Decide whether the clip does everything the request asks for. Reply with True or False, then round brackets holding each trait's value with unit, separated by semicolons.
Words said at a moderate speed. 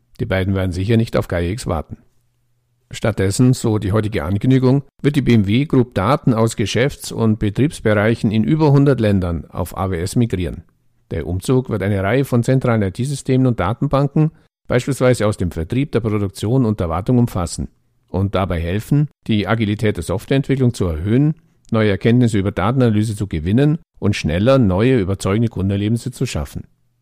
True (160 wpm)